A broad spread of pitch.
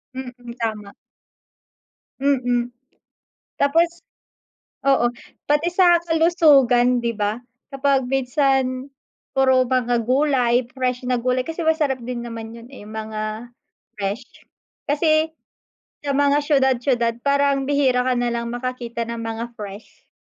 No: average, 3.0 semitones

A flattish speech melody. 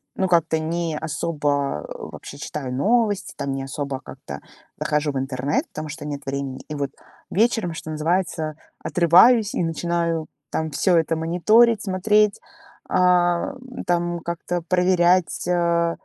No: average, 3.2 semitones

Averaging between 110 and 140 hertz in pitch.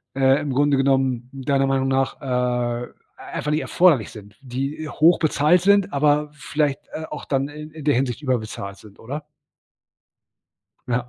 Yes: low, 135 Hz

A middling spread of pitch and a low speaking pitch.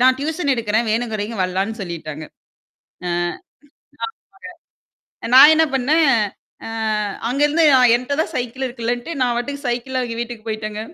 No: average, 4.0 semitones; high, 240 Hz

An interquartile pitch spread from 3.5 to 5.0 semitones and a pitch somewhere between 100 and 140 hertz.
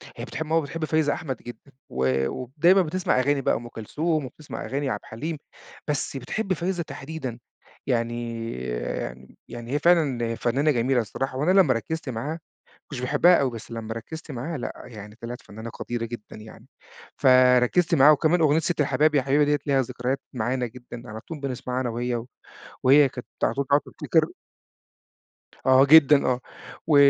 Yes: average, 4.2 semitones; low, 135 Hz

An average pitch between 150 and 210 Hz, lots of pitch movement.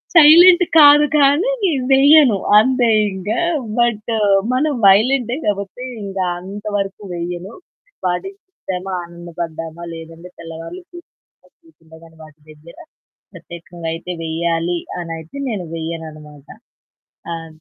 Yes: medium, 185 Hz; wide, 7.3 semitones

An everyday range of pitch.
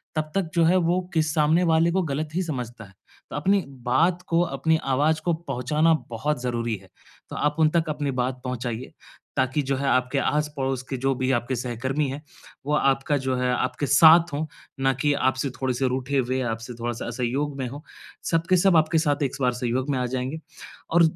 Yes: average, 3.7 semitones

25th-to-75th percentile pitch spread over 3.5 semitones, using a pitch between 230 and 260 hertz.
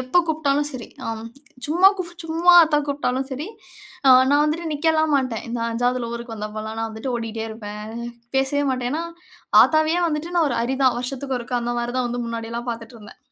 Yes: average, 4.6 semitones; very high, 255 Hz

